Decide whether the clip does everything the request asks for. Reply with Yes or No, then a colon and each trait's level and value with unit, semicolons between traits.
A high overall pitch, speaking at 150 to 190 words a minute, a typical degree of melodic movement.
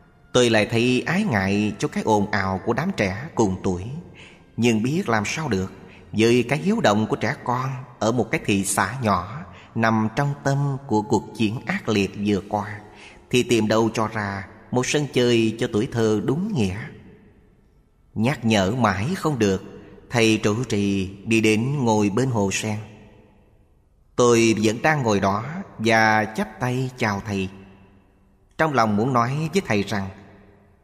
No: low, 110 Hz; slow, 165 wpm; average, 3.6 semitones